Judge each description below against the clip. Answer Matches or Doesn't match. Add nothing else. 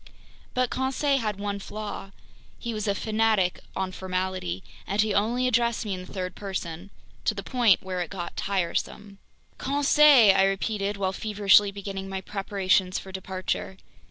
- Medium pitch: Doesn't match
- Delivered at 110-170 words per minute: Matches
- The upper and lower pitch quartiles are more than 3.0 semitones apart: Doesn't match